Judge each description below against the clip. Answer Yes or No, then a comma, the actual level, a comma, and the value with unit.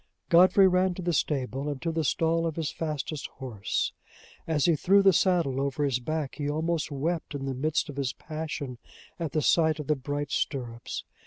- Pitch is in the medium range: Yes, medium, 150 Hz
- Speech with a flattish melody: No, average, 3.3 semitones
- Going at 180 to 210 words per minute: Yes, average, 195 wpm